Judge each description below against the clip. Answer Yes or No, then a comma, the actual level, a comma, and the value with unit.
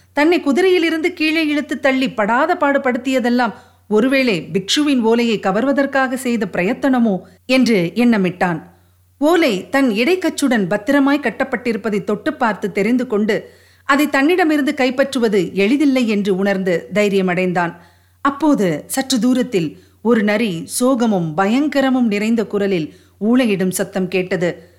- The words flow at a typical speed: Yes, average, 105 wpm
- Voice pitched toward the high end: Yes, high, 235 Hz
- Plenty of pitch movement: Yes, wide, 5.7 semitones